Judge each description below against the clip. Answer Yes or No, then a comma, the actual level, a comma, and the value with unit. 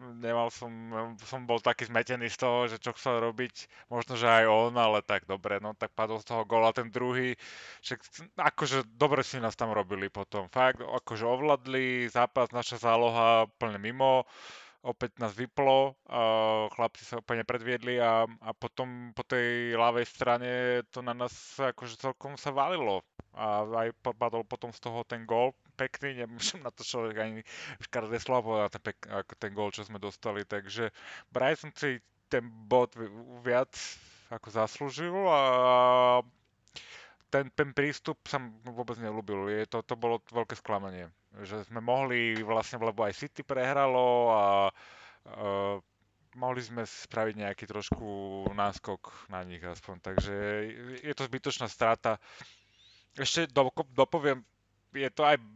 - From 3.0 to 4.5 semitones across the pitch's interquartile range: No, narrow, 2.6 semitones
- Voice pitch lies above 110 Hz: Yes, low, 120 Hz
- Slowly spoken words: No, average, 150 wpm